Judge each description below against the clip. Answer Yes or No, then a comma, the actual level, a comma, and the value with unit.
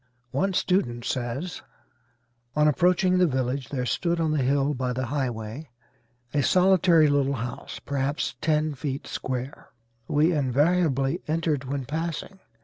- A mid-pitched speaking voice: Yes, medium, 145 Hz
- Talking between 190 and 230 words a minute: No, slow, 135 wpm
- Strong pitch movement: No, average, 4.1 semitones